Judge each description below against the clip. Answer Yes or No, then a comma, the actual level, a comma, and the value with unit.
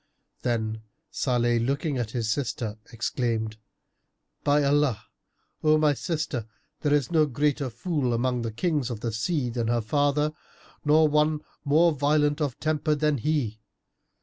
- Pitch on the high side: No, medium, 140 Hz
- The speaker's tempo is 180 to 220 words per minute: No, average, 145 wpm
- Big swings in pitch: No, average, 4.3 semitones